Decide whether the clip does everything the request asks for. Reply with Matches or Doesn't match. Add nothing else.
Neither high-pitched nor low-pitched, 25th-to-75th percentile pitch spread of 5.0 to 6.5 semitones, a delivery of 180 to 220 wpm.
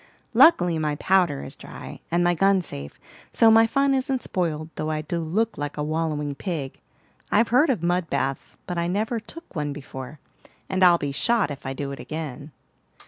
Matches